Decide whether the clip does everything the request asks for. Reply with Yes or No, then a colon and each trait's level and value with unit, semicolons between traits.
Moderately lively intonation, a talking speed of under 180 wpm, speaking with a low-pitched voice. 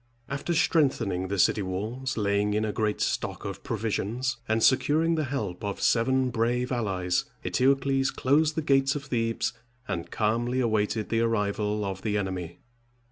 Yes: average, 4.3 semitones; average, 155 wpm; low, 115 Hz